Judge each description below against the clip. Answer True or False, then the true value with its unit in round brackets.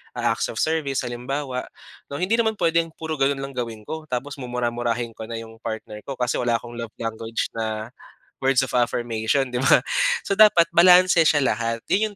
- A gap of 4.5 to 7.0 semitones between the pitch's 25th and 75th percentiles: True (5.2 semitones)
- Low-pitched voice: True (125 Hz)